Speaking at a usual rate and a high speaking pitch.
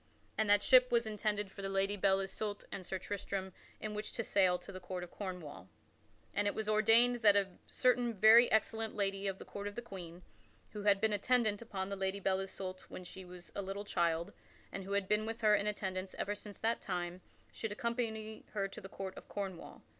No: fast, 220 wpm; high, 200 Hz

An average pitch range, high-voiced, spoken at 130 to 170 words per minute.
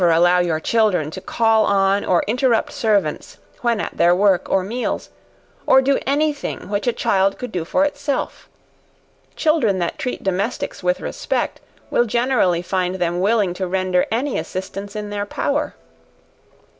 Yes: average, 4.7 semitones; high, 200 Hz; average, 160 wpm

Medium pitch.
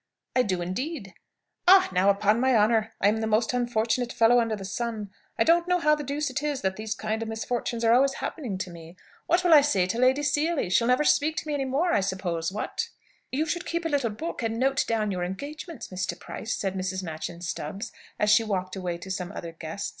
No: high, 225 Hz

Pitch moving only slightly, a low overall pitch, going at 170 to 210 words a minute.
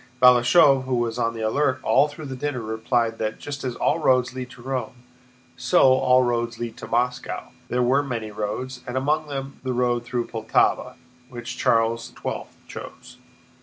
Yes: narrow, 2.0 semitones; low, 125 Hz; average, 175 wpm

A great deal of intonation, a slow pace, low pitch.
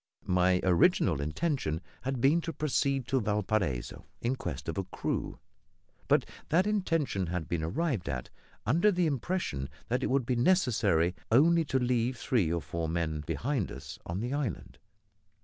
No: wide, 8.9 semitones; average, 160 wpm; low, 120 Hz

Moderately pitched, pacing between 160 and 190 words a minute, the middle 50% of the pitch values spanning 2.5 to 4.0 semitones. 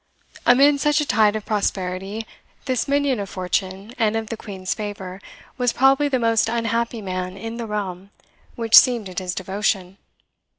No: high, 215 Hz; average, 165 wpm; average, 3.7 semitones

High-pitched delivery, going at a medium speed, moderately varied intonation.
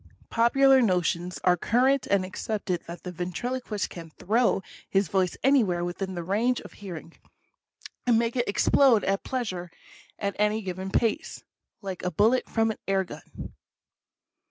Yes: high, 200 Hz; average, 155 wpm; average, 4.4 semitones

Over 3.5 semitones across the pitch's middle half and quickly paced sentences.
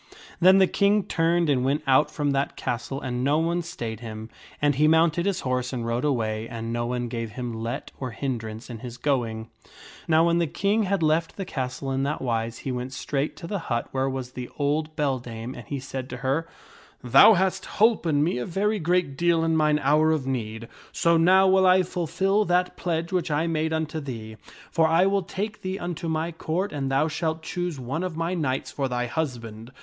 Yes: average, 5.3 semitones; fast, 215 wpm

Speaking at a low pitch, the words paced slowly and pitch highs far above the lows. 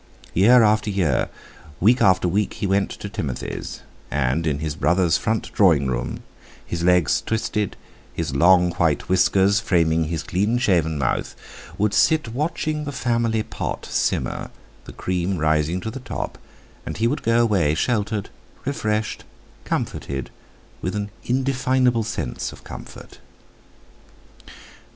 Yes: low, 100 Hz; slow, 130 wpm; wide, 5.7 semitones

